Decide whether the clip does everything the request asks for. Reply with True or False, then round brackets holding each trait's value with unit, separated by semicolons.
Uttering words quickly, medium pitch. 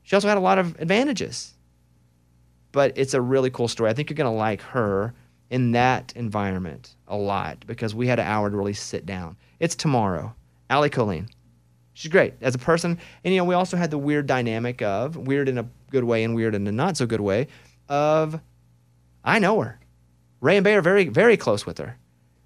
False (210 wpm; 115 Hz)